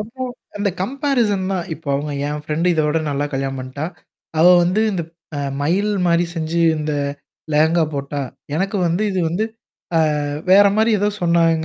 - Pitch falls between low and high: Yes, medium, 170 Hz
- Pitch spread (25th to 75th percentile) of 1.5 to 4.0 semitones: No, average, 4.7 semitones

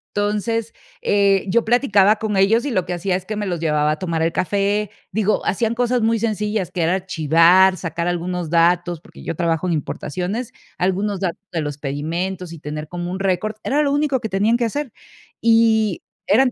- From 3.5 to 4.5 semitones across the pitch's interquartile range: Yes, average, 4.2 semitones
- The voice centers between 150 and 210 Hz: Yes, high, 190 Hz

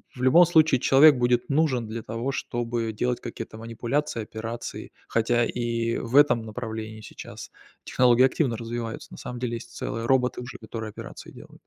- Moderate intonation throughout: No, narrow, 1.9 semitones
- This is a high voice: No, low, 120 Hz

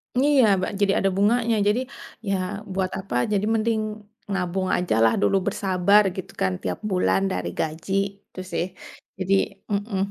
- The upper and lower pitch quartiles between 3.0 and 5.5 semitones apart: No, narrow, 2.6 semitones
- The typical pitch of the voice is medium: No, high, 195 Hz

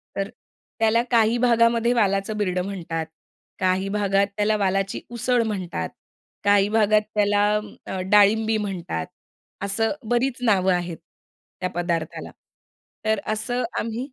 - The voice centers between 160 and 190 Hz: No, high, 205 Hz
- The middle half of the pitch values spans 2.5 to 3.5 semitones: Yes, average, 2.8 semitones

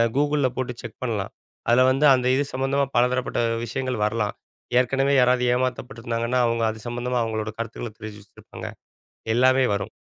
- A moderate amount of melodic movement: No, narrow, 2.1 semitones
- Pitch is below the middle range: Yes, low, 125 Hz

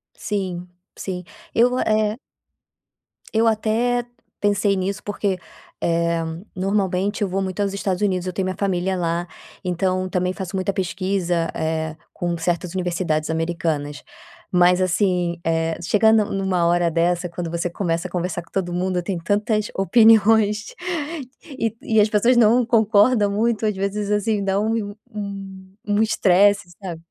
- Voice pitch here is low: No, high, 190 Hz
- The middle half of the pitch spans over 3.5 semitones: No, average, 2.9 semitones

